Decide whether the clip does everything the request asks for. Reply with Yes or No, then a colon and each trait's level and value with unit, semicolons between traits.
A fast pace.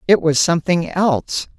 No: average, 150 wpm